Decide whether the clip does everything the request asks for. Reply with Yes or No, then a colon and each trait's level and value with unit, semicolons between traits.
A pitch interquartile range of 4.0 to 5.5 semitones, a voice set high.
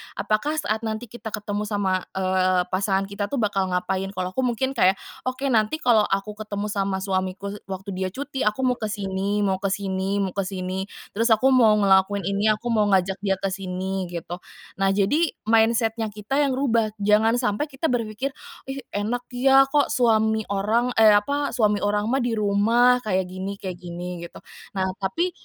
No: average, 3.5 semitones; high, 210 Hz